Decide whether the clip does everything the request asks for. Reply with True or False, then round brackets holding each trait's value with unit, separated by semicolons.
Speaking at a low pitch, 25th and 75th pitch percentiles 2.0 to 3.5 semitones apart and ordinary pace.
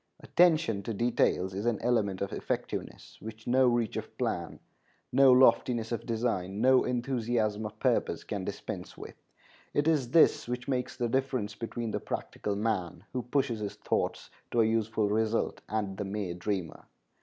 True (115 Hz; 3.1 semitones; 165 wpm)